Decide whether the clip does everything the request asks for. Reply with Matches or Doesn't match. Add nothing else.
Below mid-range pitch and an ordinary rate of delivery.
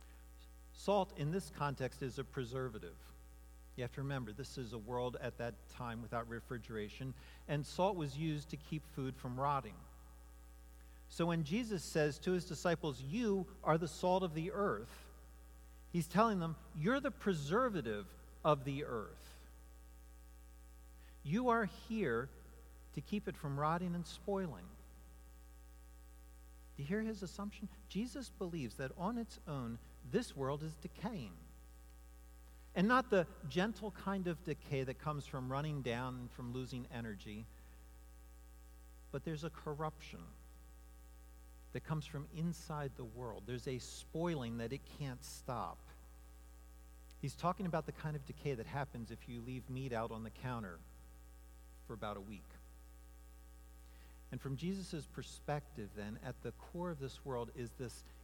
Matches